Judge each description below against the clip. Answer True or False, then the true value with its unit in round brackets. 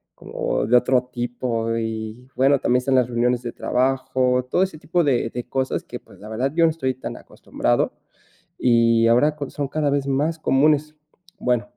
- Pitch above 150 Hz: False (125 Hz)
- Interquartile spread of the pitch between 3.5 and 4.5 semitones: False (2.7 semitones)